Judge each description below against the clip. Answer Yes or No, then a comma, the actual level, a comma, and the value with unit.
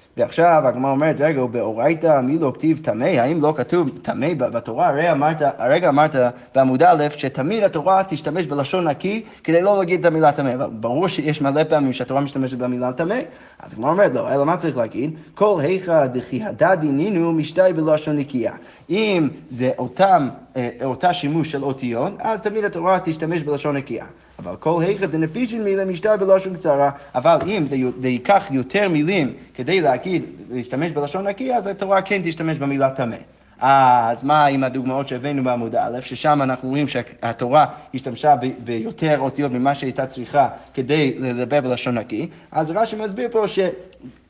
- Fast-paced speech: Yes, fast, 160 wpm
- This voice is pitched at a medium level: Yes, medium, 150 Hz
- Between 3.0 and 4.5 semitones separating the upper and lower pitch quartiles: No, wide, 5.5 semitones